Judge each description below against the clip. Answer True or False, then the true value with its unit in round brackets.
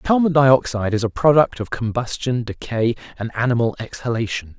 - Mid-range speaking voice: False (120 Hz)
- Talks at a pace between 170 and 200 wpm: False (145 wpm)